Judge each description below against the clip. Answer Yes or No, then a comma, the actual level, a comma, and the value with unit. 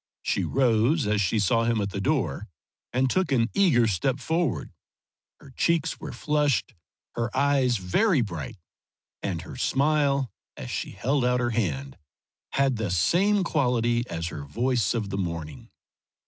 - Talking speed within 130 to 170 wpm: Yes, average, 155 wpm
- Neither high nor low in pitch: No, low, 120 Hz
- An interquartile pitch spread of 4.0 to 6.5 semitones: Yes, wide, 5.6 semitones